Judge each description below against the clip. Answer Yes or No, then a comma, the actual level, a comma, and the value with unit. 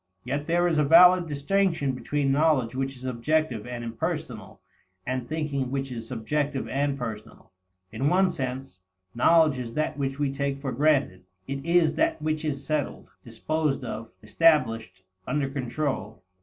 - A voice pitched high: No, medium, 140 Hz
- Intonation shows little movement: No, average, 3.5 semitones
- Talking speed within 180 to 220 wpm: No, average, 155 wpm